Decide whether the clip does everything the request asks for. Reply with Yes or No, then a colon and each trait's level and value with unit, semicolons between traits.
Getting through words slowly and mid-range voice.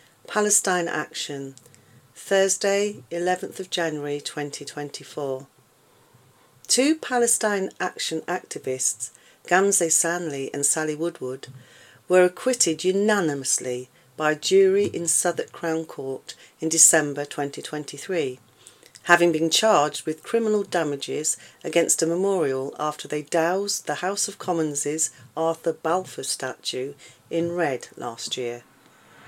Yes: slow, 105 wpm; medium, 160 Hz